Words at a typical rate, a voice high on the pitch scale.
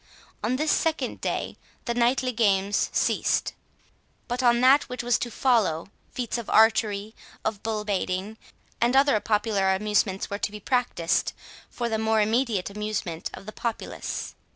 Yes: average, 155 wpm; high, 220 Hz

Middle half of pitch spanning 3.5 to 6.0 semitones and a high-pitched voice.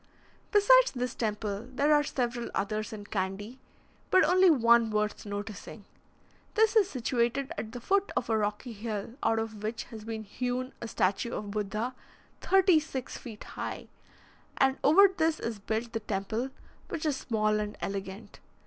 Yes: average, 4.2 semitones; high, 230 Hz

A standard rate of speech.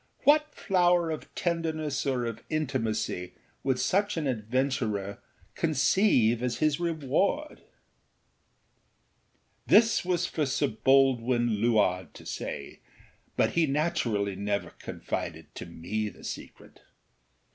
No: slow, 110 wpm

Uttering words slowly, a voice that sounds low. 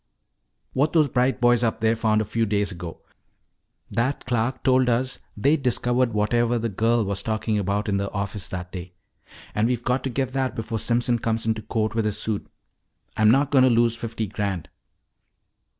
No: average, 190 wpm; low, 115 Hz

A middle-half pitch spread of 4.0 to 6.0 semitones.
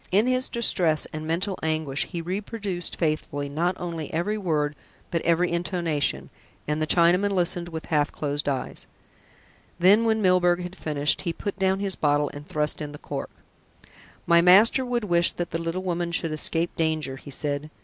No: average, 3.3 semitones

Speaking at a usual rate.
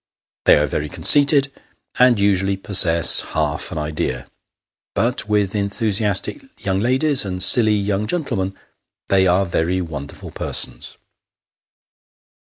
No: slow, 115 wpm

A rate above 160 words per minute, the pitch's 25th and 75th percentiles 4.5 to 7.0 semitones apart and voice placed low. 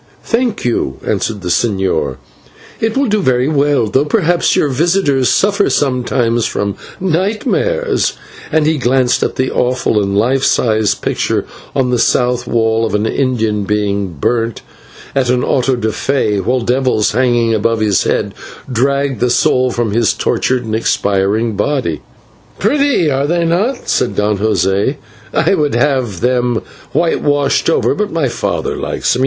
No: average, 155 wpm; average, 4.9 semitones; low, 125 Hz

